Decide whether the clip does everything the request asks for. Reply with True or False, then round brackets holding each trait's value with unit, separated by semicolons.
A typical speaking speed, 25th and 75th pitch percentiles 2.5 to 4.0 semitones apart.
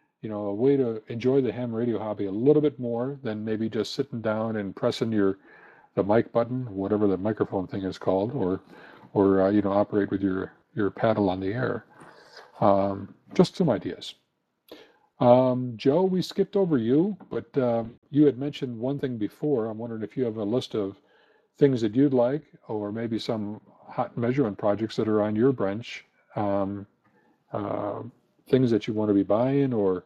False (190 wpm; 4.4 semitones)